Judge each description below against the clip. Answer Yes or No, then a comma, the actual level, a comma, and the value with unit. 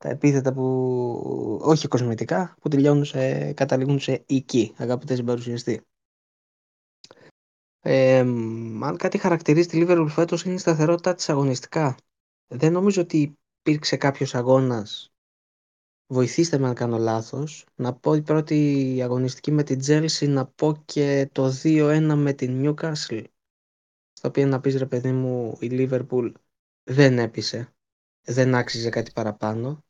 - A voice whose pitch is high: No, low, 135 Hz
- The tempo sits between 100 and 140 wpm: Yes, average, 130 wpm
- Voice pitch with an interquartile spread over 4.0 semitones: No, average, 3.5 semitones